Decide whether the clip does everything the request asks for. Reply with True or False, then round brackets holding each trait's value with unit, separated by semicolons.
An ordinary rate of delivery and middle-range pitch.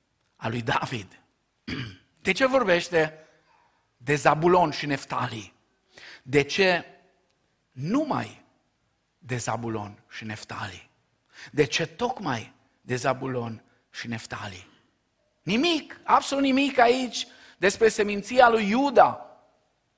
False (95 wpm; 155 Hz)